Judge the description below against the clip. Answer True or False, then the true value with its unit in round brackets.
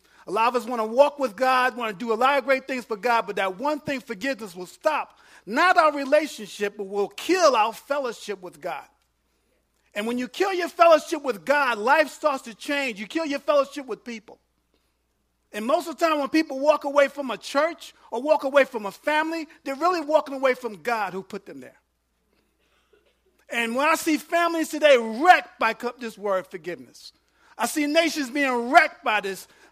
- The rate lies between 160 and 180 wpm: False (200 wpm)